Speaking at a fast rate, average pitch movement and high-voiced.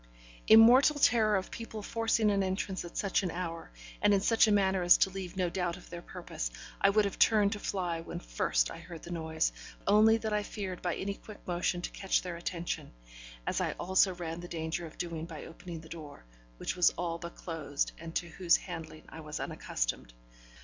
No: fast, 210 wpm; average, 3.3 semitones; medium, 180 Hz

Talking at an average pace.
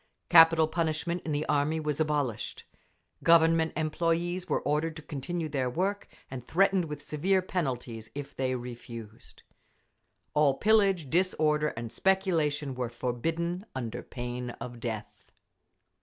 No: slow, 125 wpm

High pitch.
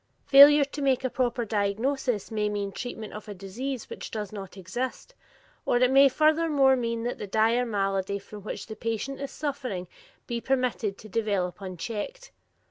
Yes: high, 230 Hz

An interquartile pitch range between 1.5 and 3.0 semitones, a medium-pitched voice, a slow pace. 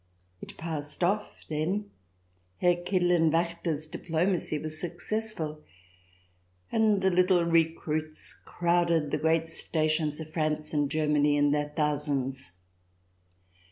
Yes: narrow, 2.5 semitones; medium, 160 Hz; slow, 110 wpm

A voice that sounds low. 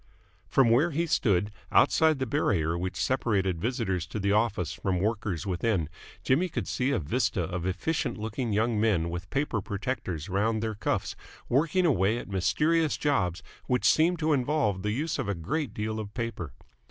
Yes: low, 110 Hz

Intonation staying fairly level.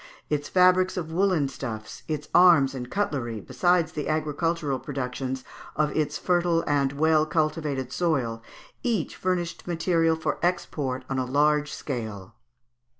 No: average, 4.1 semitones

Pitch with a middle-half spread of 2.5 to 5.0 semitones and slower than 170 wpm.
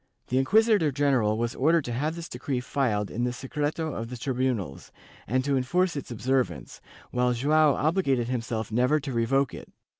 No: average, 3.6 semitones; average, 175 wpm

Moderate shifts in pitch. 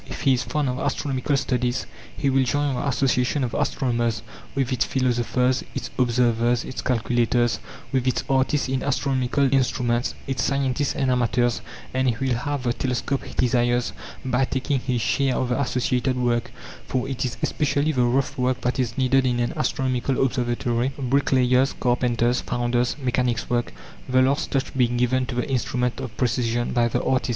No: narrow, 1.6 semitones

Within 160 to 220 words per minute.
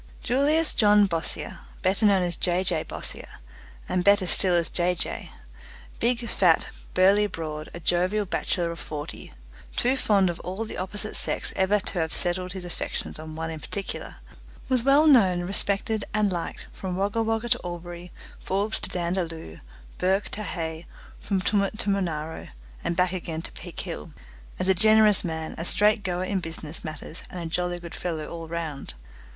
Yes: average, 175 wpm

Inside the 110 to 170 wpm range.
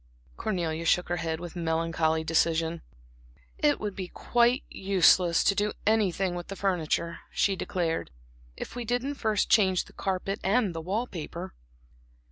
Yes: average, 150 wpm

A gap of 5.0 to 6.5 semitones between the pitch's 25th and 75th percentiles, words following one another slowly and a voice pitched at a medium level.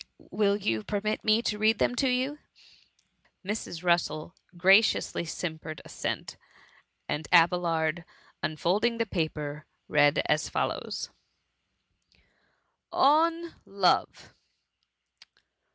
Yes: wide, 5.6 semitones; slow, 100 wpm; medium, 180 Hz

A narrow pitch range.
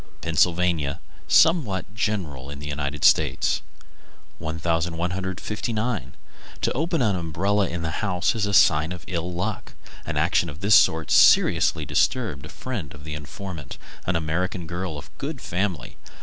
No: average, 4.5 semitones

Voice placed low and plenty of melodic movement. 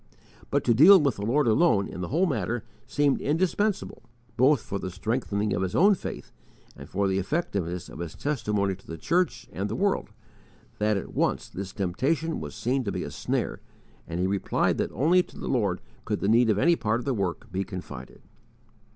Yes: low, 110 Hz; wide, 7.1 semitones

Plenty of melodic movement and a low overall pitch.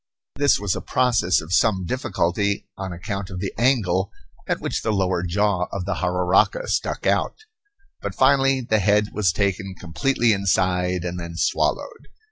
No: average, 3.3 semitones; very low, 95 Hz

